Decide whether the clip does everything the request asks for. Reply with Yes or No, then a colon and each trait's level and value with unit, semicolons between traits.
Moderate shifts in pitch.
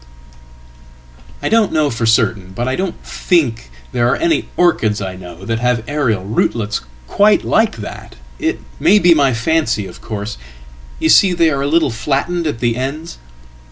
No: wide, 6.6 semitones